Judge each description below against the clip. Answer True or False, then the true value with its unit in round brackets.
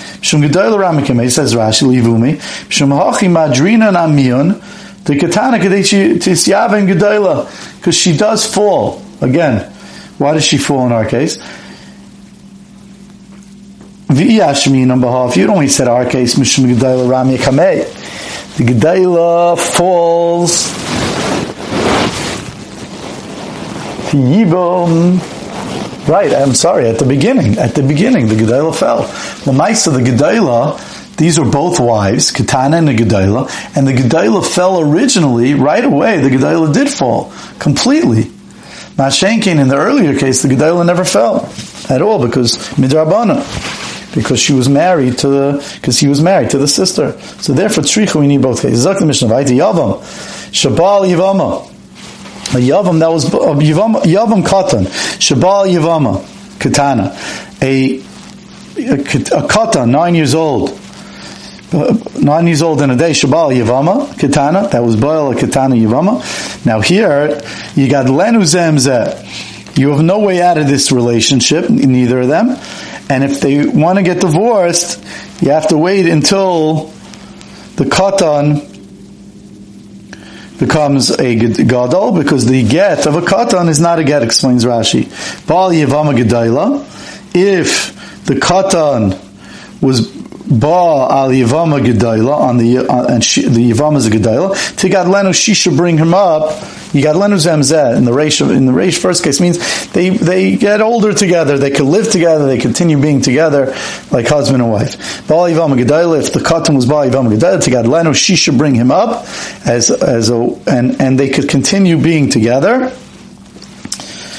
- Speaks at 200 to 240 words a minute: False (140 wpm)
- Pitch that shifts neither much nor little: False (5.7 semitones)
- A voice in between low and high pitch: True (150 Hz)